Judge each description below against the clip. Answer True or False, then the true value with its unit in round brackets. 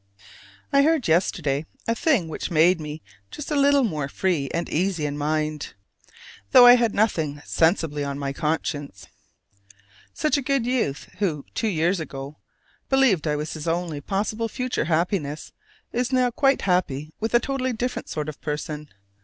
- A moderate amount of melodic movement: False (8.0 semitones)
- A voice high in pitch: False (170 Hz)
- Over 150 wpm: True (160 wpm)